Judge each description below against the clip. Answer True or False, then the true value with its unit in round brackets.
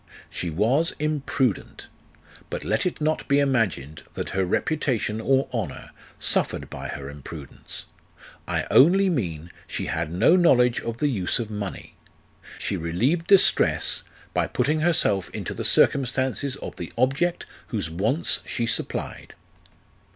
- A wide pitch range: True (7.6 semitones)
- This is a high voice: False (125 Hz)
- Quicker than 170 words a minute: False (135 wpm)